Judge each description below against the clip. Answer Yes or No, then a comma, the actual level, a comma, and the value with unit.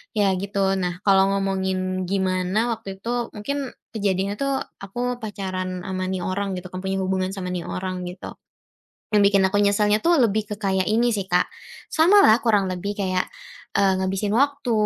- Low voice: No, high, 195 Hz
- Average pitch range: No, narrow, 2.2 semitones